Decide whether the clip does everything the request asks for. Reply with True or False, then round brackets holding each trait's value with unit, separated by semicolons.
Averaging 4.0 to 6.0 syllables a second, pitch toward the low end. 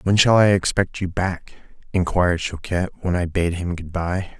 True (5.0 syllables/s; 90 Hz)